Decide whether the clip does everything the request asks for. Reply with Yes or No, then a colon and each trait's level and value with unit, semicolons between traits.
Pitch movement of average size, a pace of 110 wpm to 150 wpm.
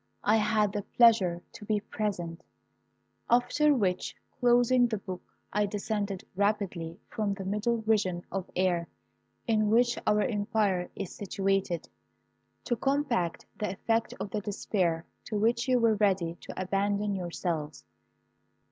Yes: average, 3.1 semitones; slow, 135 wpm